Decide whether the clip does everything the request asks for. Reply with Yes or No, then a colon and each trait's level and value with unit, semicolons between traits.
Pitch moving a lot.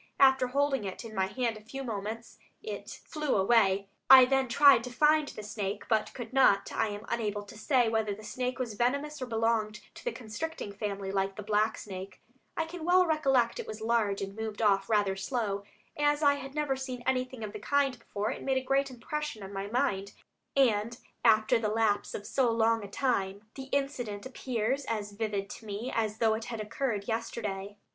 No: average, 4.3 semitones